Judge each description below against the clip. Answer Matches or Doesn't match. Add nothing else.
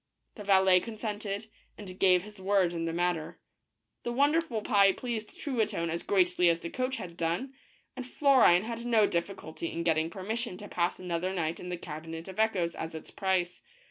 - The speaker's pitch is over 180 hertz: Matches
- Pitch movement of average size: Matches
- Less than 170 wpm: Doesn't match